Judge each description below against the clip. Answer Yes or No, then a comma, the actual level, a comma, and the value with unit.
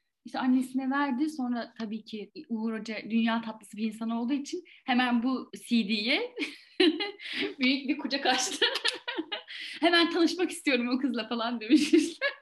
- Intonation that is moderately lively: No, wide, 6.0 semitones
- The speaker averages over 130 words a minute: Yes, fast, 140 wpm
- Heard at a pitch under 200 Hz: No, very high, 265 Hz